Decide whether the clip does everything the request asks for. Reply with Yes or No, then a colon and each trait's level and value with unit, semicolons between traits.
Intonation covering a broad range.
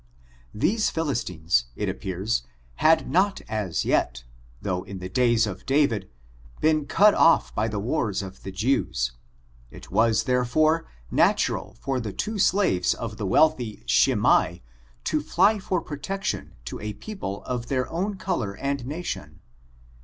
Yes: wide, 8.3 semitones